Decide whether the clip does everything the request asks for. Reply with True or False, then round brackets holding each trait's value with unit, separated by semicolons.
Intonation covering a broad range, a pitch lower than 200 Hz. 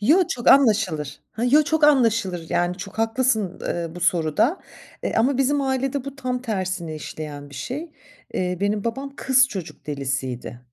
False (7.8 semitones; 215 Hz)